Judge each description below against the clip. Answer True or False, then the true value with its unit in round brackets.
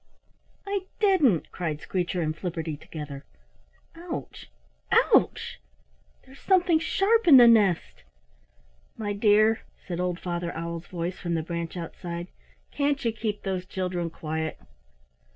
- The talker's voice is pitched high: False (180 Hz)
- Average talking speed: False (125 wpm)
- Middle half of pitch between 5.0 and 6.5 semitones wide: True (5.5 semitones)